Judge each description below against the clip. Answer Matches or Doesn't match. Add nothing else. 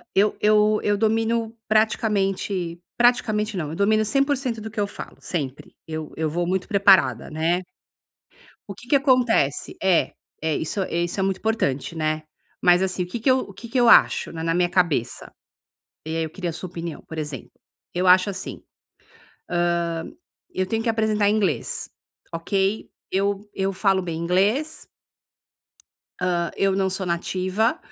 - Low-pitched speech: Doesn't match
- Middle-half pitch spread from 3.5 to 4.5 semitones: Matches